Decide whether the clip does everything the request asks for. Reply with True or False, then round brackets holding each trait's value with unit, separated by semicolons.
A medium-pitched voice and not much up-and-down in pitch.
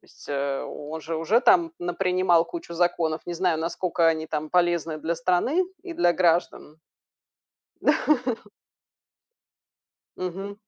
True (175 Hz; 2.3 semitones)